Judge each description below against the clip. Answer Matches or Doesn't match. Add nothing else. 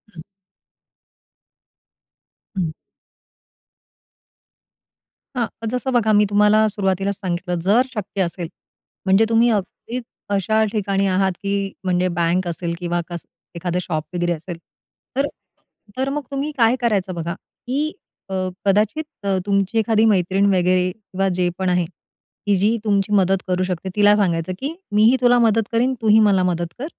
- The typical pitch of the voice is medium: Doesn't match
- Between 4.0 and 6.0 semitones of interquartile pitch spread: Doesn't match